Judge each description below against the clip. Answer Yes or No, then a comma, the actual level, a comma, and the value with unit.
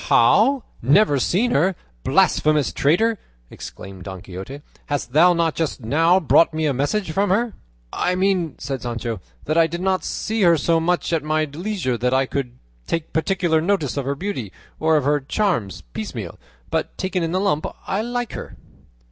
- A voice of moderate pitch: Yes, medium, 160 Hz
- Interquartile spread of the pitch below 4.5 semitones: No, average, 5.3 semitones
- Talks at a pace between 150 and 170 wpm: No, average, 180 wpm